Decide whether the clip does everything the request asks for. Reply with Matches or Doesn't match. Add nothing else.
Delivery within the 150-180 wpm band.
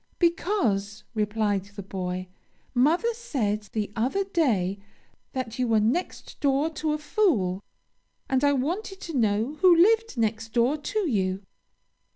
Doesn't match